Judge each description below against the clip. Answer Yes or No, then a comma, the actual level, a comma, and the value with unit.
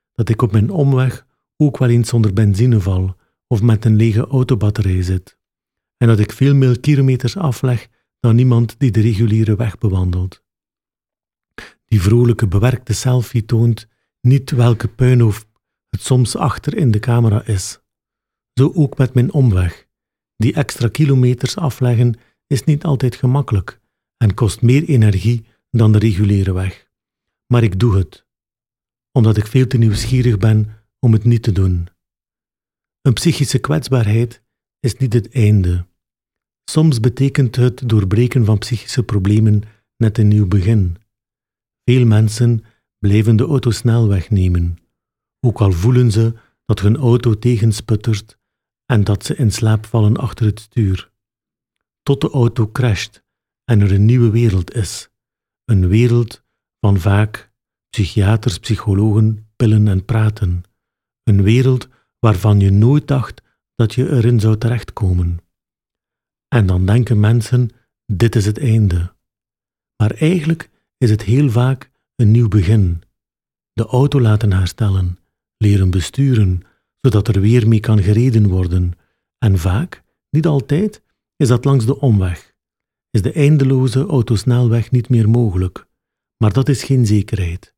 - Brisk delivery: No, average, 140 wpm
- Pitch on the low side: Yes, low, 115 Hz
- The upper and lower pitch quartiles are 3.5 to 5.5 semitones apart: No, average, 2.9 semitones